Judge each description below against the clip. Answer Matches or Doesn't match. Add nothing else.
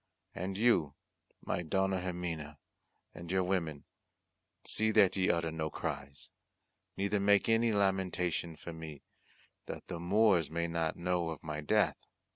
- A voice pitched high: Doesn't match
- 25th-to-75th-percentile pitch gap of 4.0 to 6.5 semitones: Doesn't match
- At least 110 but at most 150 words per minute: Matches